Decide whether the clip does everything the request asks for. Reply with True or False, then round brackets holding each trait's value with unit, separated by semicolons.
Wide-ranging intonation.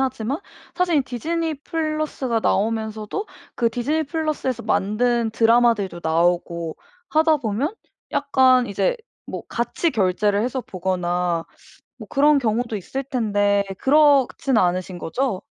True (5.9 semitones)